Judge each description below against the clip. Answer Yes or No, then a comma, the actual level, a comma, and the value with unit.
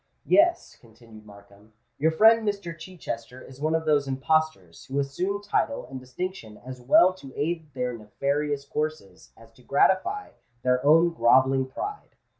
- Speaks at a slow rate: No, average, 150 wpm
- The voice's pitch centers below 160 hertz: Yes, medium, 140 Hz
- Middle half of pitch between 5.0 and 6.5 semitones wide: Yes, average, 5.3 semitones